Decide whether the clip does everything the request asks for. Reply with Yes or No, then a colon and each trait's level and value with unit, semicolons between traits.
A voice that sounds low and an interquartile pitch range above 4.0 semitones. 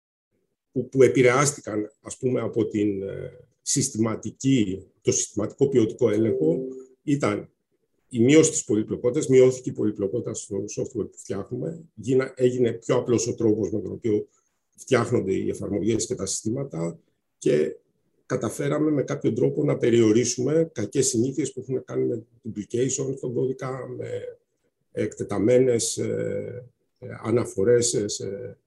No: low, 125 Hz; average, 3.5 semitones